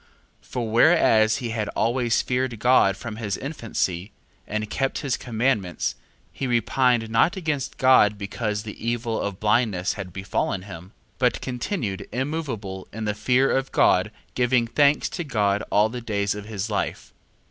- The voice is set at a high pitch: No, low, 115 Hz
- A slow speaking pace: No, average, 160 wpm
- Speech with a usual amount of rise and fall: Yes, average, 3.6 semitones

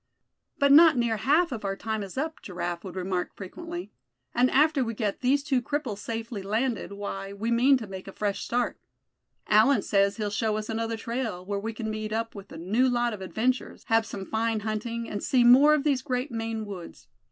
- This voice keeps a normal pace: No, fast, 210 wpm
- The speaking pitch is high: Yes, high, 225 Hz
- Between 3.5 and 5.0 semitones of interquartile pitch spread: Yes, average, 3.9 semitones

